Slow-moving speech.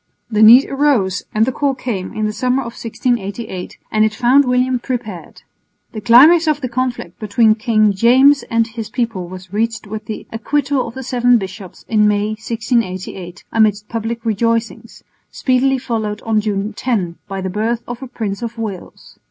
No: average, 175 wpm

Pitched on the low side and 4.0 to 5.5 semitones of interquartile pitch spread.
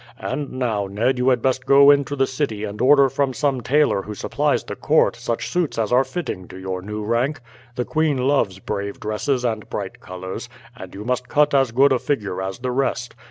Yes: low, 125 Hz; average, 4.6 semitones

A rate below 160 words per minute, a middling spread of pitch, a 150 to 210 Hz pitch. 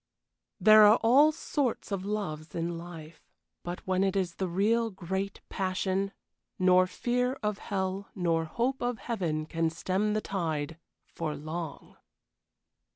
Yes: average, 140 wpm; average, 4.1 semitones; high, 190 Hz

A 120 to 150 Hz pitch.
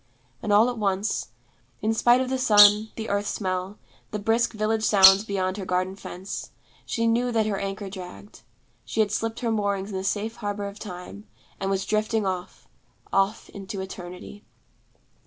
No: high, 205 Hz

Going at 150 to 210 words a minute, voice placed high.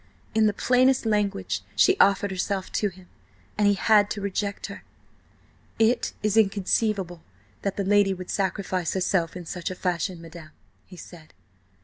Yes: average, 155 wpm; high, 195 Hz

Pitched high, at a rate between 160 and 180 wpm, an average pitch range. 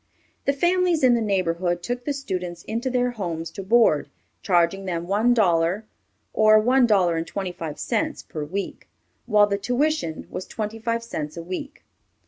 No: high, 205 Hz; average, 170 wpm; wide, 5.8 semitones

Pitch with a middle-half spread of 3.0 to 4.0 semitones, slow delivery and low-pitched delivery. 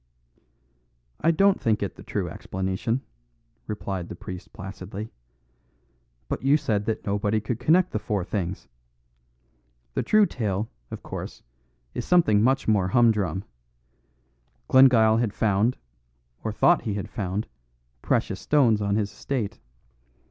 Yes: average, 3.5 semitones; slow, 130 wpm; low, 110 Hz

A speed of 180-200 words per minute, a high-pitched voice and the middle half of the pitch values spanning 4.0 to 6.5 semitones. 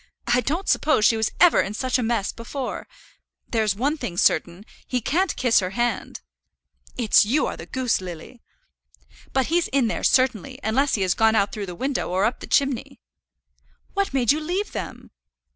Yes: average, 185 wpm; high, 240 Hz; average, 4.6 semitones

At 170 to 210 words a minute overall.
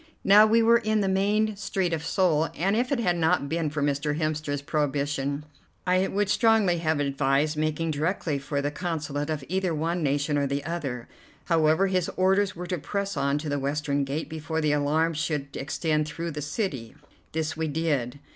Yes: average, 190 wpm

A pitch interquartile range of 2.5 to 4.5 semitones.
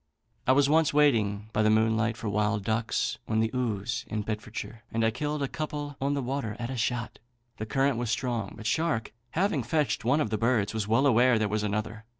Yes: average, 4.0 semitones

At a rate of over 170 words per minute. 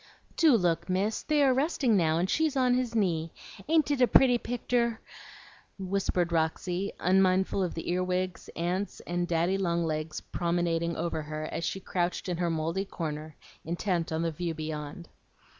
No: average, 165 wpm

